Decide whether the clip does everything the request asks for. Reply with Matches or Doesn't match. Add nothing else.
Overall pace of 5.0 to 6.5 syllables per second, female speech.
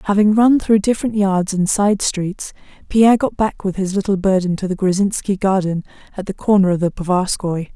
Matches